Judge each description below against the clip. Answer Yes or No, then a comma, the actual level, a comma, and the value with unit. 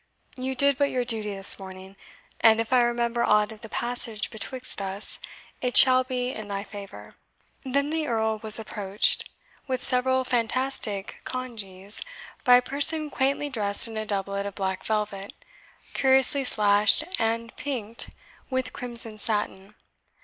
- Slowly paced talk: No, average, 150 wpm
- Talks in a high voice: Yes, high, 230 Hz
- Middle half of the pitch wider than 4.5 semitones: No, average, 3.7 semitones